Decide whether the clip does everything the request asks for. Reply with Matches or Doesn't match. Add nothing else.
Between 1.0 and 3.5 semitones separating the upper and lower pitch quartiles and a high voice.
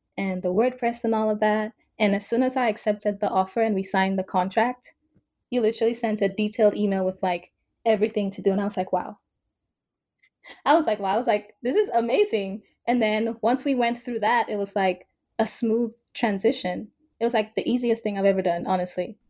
Matches